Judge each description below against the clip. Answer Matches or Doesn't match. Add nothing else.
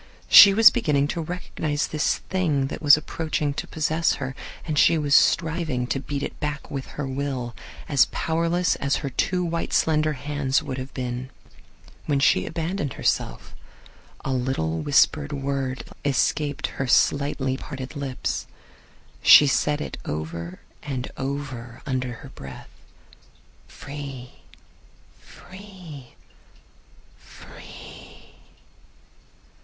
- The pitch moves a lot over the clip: Doesn't match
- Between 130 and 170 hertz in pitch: Matches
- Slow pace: Matches